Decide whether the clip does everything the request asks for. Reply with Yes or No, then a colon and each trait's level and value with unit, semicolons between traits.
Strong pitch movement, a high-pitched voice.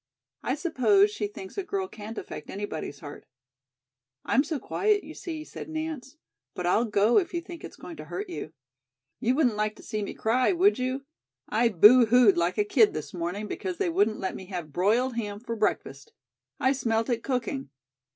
Yes: wide, 7.3 semitones; high, 235 Hz